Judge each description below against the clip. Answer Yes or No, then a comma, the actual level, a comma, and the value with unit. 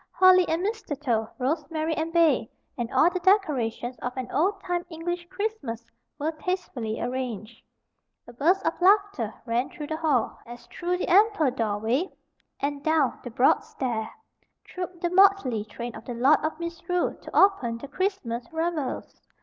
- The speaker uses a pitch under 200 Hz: No, very high, 310 Hz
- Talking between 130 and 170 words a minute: Yes, average, 160 wpm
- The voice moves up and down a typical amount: No, wide, 6.7 semitones